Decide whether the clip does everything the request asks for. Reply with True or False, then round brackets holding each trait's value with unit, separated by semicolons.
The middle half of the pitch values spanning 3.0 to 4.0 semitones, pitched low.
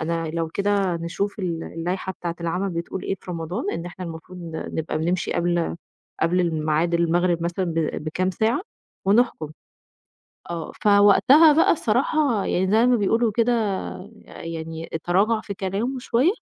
False (3.5 semitones; 180 Hz)